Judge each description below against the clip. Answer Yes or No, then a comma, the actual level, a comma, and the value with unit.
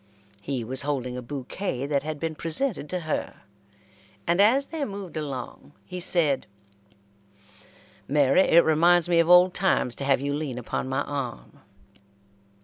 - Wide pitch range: No, average, 4.7 semitones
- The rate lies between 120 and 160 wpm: Yes, average, 150 wpm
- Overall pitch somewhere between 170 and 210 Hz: No, medium, 150 Hz